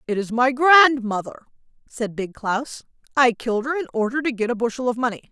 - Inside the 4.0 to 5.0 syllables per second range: No, 5.6 syllables/s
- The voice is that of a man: No, female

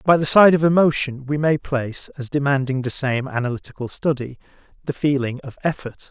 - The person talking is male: Yes, male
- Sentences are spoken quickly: No, average, 175 wpm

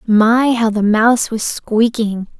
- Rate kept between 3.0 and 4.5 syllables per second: Yes, 3.7 syllables/s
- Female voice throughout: Yes, female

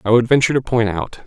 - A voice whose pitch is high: No, low, 120 Hz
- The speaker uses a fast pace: Yes, fast, 285 wpm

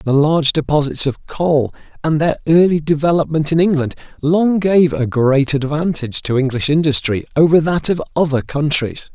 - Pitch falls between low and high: Yes, medium, 150 Hz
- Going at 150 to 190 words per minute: Yes, average, 155 wpm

